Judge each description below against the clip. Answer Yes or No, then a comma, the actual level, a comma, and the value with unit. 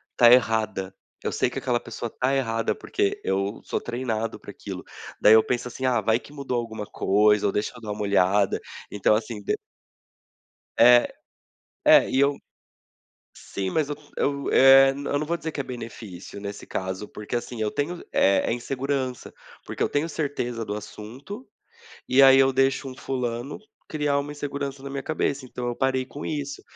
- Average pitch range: Yes, average, 4.2 semitones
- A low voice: Yes, low, 125 Hz